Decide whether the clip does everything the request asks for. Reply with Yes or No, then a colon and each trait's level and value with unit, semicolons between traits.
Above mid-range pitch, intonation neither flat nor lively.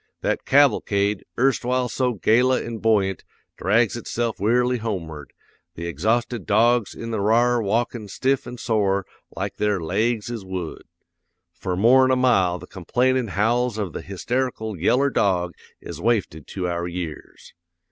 No: low, 110 Hz; average, 4.3 semitones